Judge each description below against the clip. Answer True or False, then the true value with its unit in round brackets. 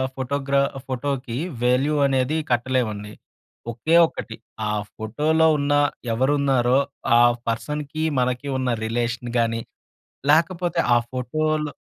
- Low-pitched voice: True (130 Hz)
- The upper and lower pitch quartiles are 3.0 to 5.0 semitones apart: True (3.5 semitones)